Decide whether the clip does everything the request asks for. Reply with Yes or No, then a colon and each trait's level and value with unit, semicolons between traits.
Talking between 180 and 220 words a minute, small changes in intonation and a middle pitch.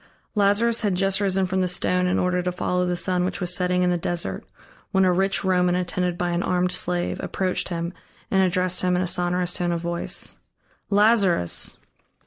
Yes: average, 195 wpm; narrow, 1.1 semitones; medium, 180 Hz